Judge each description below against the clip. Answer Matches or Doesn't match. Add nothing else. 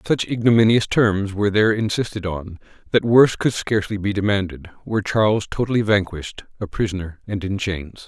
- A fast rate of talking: Doesn't match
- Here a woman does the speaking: Doesn't match